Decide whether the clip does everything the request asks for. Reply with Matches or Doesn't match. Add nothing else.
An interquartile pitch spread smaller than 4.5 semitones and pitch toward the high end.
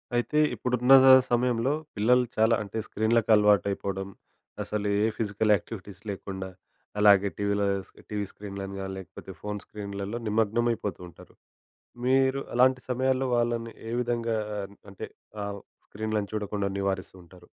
Doesn't match